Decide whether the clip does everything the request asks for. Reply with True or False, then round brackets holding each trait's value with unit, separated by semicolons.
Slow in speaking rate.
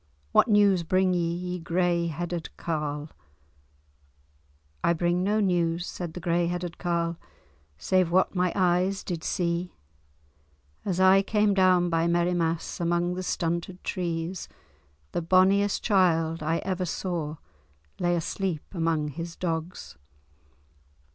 True (125 wpm)